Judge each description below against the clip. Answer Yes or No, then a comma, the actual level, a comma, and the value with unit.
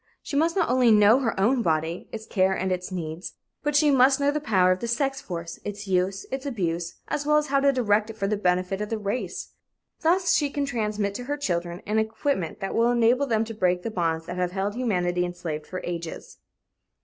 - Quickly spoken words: Yes, fast, 225 wpm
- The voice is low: No, high, 210 Hz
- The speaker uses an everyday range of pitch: No, wide, 6.2 semitones